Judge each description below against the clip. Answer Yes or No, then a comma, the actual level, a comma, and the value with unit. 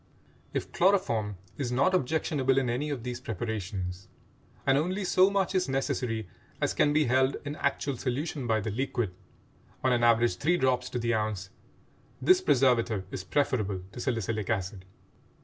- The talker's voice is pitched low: Yes, low, 125 Hz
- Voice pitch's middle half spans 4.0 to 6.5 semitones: Yes, average, 4.5 semitones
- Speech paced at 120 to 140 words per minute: No, average, 150 wpm